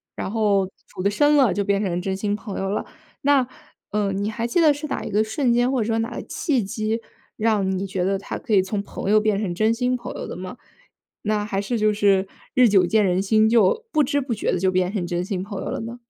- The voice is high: Yes, high, 210 Hz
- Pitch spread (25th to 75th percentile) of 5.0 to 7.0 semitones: No, average, 3.2 semitones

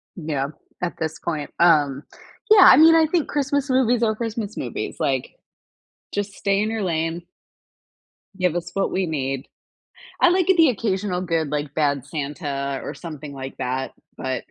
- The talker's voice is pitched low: No, medium, 175 Hz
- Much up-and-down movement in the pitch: Yes, wide, 7.4 semitones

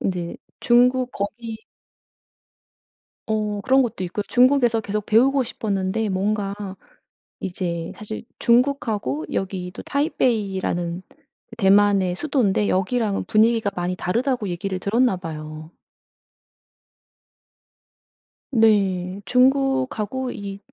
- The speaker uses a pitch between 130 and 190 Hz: No, high, 210 Hz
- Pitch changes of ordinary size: Yes, average, 4.4 semitones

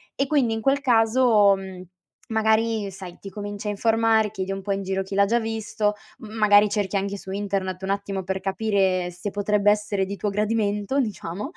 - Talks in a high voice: Yes, high, 205 Hz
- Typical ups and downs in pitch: No, narrow, 2.2 semitones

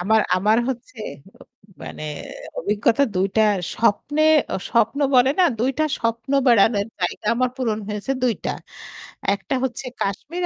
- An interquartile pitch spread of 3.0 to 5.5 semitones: Yes, average, 3.7 semitones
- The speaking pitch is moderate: No, high, 230 Hz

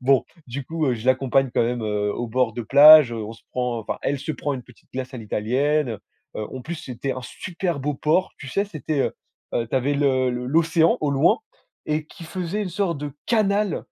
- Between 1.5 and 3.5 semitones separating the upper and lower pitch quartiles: No, average, 4.2 semitones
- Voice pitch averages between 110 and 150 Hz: Yes, low, 135 Hz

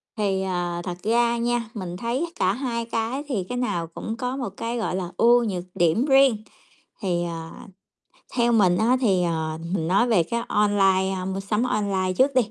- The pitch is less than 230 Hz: Yes, high, 210 Hz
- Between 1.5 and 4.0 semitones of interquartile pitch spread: No, average, 4.5 semitones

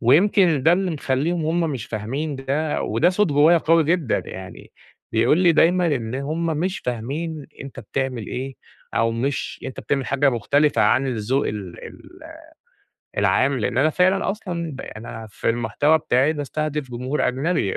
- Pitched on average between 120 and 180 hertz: Yes, medium, 140 Hz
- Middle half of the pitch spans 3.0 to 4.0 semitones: No, average, 4.6 semitones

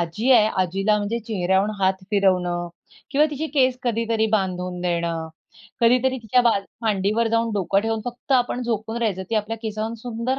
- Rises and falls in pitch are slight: No, average, 3.7 semitones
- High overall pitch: Yes, high, 220 Hz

